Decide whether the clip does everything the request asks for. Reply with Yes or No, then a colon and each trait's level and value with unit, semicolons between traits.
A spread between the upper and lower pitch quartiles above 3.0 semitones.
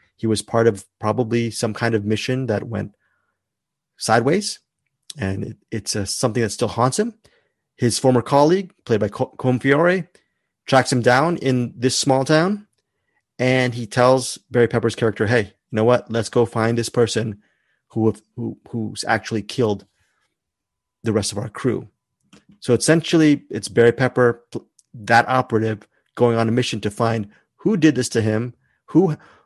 No: narrow, 2.6 semitones